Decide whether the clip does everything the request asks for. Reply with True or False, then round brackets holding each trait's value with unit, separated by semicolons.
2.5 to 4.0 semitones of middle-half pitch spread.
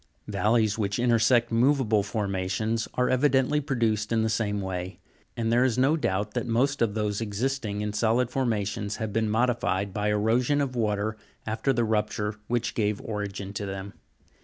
True (2.8 semitones)